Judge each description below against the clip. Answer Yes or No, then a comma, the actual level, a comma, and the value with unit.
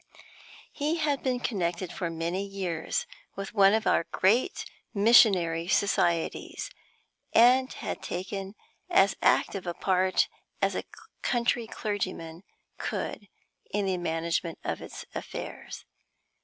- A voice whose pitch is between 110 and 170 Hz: No, high, 195 Hz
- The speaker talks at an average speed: No, slow, 115 wpm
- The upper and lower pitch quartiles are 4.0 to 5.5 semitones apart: Yes, average, 4.3 semitones